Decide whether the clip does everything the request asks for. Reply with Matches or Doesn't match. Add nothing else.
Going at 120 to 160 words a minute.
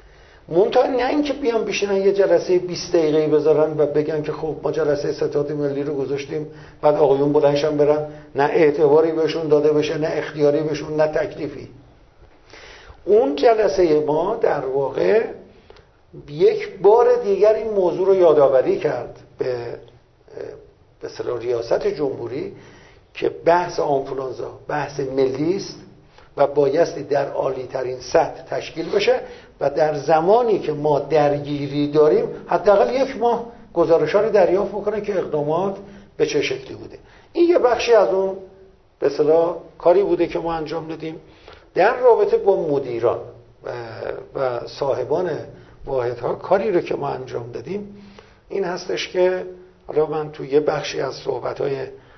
Matches